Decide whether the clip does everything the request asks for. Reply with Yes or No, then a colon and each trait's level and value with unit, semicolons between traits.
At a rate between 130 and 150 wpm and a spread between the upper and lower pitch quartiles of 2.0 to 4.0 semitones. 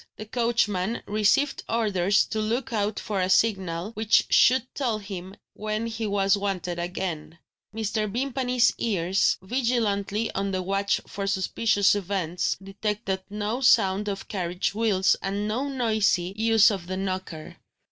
Yes: average, 140 wpm; average, 2.8 semitones